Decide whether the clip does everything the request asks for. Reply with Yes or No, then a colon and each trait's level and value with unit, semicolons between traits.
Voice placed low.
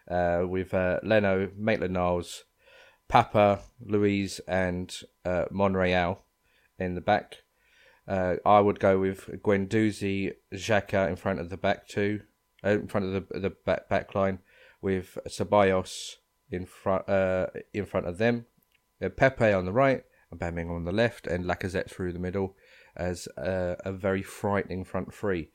Yes: very low, 95 Hz